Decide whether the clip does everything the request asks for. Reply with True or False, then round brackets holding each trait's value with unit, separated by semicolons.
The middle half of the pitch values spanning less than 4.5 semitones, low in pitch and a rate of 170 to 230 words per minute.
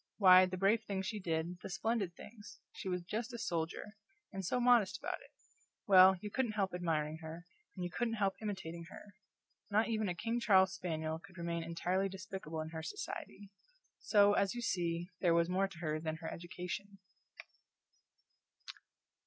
False (3.5 semitones; 185 Hz; 175 wpm)